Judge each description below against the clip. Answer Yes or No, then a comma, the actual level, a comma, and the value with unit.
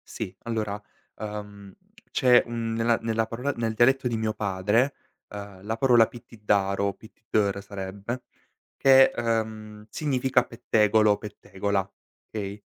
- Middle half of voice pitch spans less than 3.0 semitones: Yes, narrow, 2.5 semitones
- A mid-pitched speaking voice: No, low, 110 Hz